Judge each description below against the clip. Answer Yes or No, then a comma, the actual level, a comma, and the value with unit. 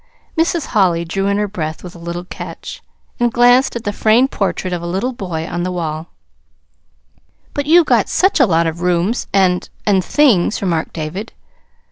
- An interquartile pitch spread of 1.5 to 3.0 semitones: No, wide, 5.5 semitones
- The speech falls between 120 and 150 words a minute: No, average, 180 wpm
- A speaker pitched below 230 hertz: Yes, high, 190 Hz